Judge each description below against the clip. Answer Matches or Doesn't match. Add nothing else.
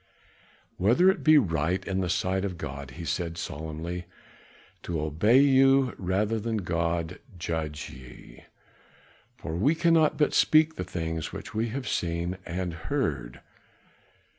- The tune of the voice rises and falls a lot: Matches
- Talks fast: Doesn't match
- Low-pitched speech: Matches